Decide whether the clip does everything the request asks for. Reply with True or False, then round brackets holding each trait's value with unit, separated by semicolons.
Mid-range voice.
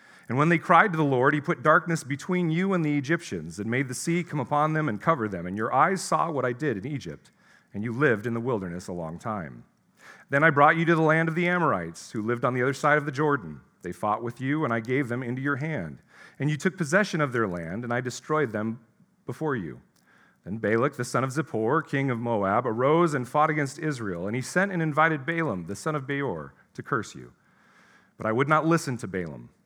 True (145 Hz)